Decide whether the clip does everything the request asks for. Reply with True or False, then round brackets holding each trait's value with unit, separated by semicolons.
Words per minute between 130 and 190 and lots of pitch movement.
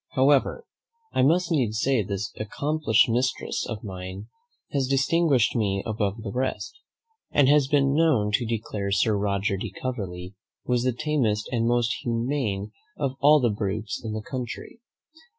False (150 wpm; 4.7 semitones)